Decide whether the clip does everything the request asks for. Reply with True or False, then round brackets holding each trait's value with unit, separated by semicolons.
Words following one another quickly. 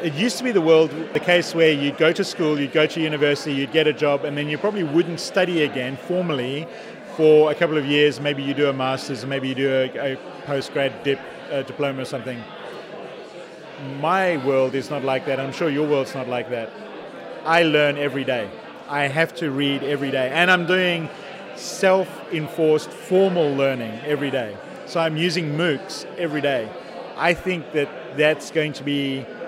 False (195 wpm)